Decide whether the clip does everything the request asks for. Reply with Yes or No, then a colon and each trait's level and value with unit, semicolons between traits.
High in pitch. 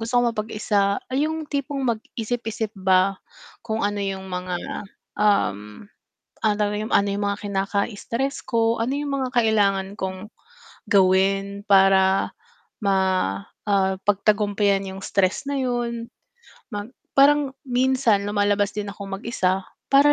Yes: high, 205 Hz